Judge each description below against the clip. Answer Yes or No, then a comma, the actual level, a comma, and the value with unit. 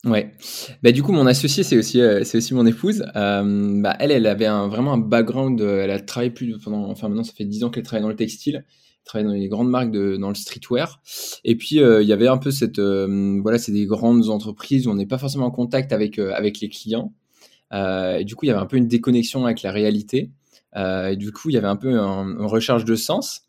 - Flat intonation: No, average, 3.2 semitones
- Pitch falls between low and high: No, low, 110 Hz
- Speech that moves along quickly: Yes, fast, 260 wpm